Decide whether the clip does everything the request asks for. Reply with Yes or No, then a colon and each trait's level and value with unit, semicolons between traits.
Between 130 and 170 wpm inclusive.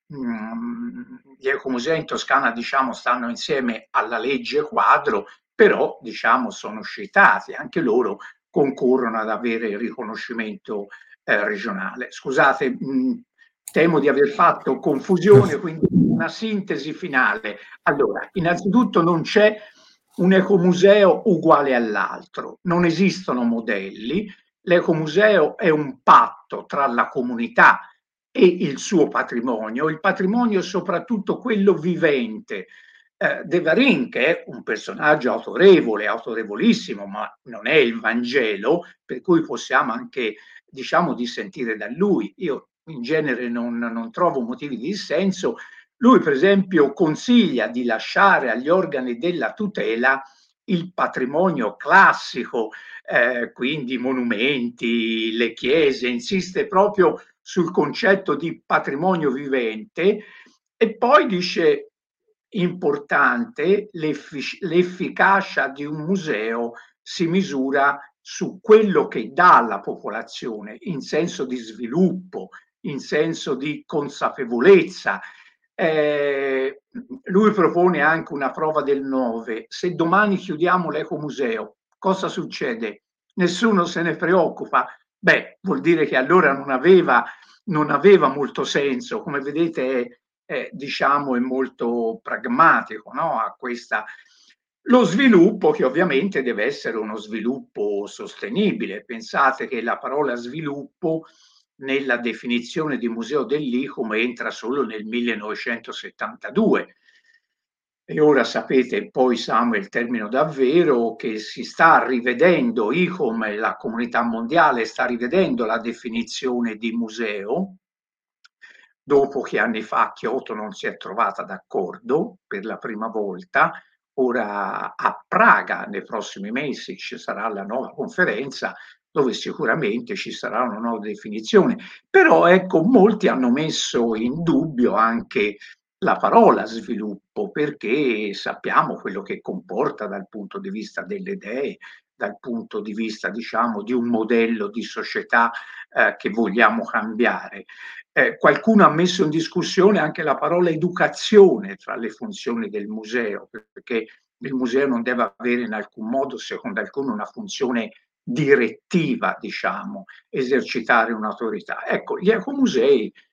No: average, 120 wpm